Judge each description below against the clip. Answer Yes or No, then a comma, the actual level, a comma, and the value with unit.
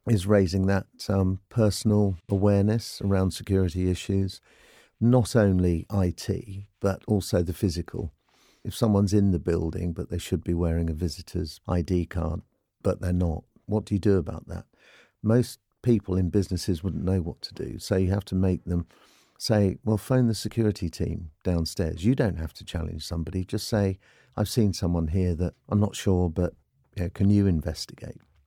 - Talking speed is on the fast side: No, average, 175 wpm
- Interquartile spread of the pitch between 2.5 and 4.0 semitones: Yes, average, 2.9 semitones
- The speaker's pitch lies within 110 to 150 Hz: No, very low, 95 Hz